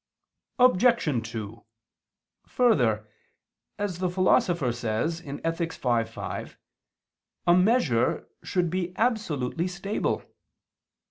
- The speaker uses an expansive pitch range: Yes, wide, 7.3 semitones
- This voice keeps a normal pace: No, slow, 85 wpm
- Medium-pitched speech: Yes, medium, 170 Hz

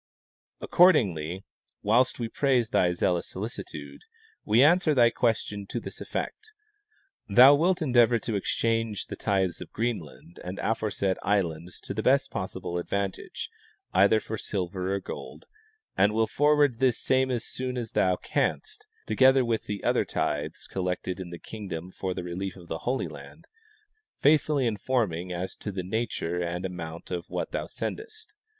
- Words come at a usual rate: Yes, average, 155 wpm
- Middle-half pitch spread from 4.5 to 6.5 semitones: Yes, wide, 5.5 semitones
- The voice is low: Yes, low, 105 Hz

